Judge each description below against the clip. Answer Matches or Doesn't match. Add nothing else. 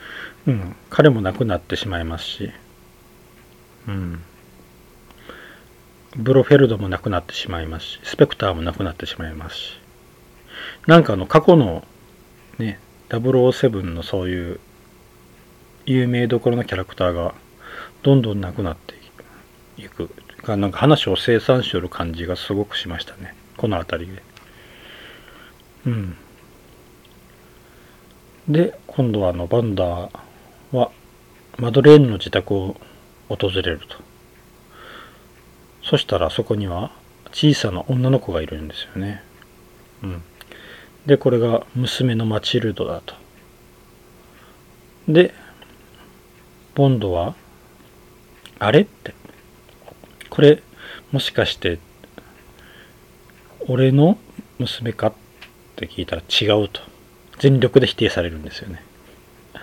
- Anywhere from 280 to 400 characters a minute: Doesn't match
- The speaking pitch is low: Matches